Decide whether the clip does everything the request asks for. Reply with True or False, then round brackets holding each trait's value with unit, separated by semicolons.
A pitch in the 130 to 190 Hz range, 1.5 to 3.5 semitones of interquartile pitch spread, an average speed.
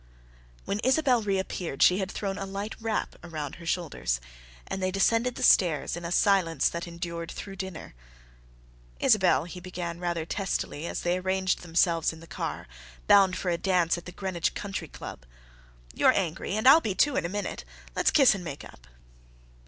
True (185 Hz; 2.6 semitones; 180 wpm)